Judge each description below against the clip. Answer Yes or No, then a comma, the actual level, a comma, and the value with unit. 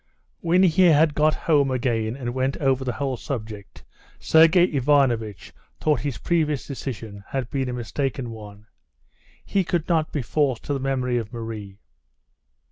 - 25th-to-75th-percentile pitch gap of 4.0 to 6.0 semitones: Yes, average, 4.5 semitones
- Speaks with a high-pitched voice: No, low, 135 Hz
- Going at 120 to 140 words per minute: No, average, 155 wpm